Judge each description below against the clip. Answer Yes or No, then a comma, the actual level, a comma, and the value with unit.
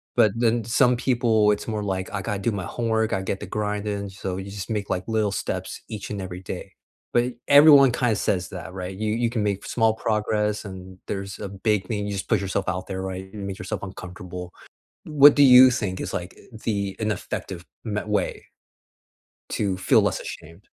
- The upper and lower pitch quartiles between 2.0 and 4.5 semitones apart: Yes, average, 2.8 semitones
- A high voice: No, low, 105 Hz